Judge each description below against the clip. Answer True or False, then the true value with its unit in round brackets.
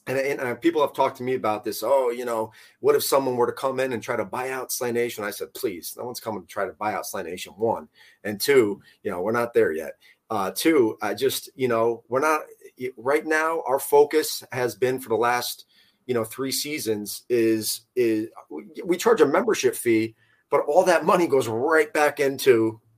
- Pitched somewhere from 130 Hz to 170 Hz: True (140 Hz)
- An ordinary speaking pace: False (220 wpm)